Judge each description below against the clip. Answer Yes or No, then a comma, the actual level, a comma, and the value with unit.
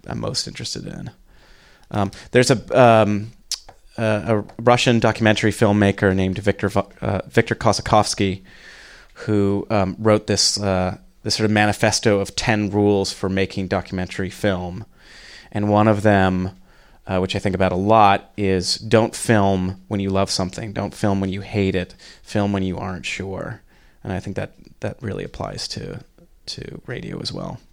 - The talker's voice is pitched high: No, low, 100 Hz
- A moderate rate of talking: Yes, average, 160 wpm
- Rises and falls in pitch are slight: Yes, narrow, 2.1 semitones